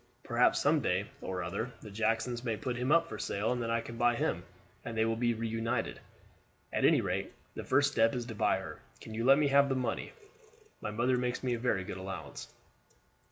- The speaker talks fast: Yes, fast, 220 wpm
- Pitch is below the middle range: Yes, low, 115 Hz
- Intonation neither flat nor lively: No, narrow, 2.3 semitones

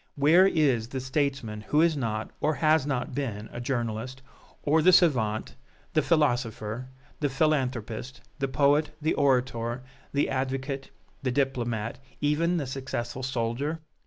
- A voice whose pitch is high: No, low, 130 Hz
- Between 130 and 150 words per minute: Yes, slow, 135 wpm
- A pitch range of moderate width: Yes, average, 3.6 semitones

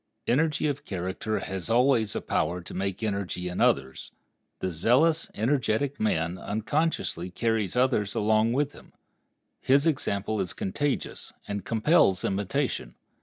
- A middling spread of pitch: No, wide, 6.1 semitones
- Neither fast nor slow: No, slow, 130 wpm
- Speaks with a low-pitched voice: Yes, low, 110 Hz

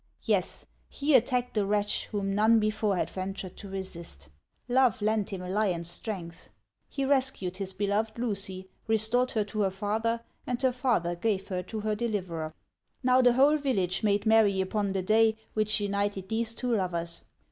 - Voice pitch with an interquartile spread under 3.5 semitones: Yes, average, 3.1 semitones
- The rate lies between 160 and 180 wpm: Yes, average, 170 wpm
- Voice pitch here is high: Yes, high, 210 Hz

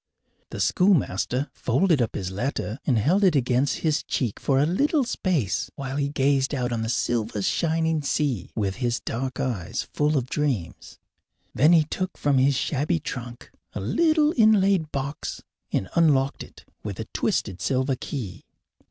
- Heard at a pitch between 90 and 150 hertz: Yes, medium, 140 Hz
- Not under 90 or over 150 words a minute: No, average, 160 wpm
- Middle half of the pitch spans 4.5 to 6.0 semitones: Yes, average, 4.8 semitones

